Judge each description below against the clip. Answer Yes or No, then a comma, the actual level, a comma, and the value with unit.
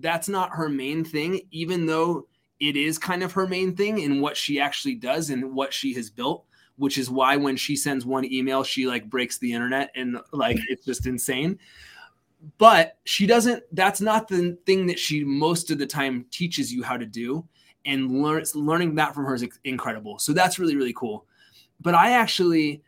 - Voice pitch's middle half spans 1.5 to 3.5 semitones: No, average, 4.8 semitones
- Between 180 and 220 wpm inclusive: Yes, average, 200 wpm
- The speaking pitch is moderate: Yes, medium, 150 Hz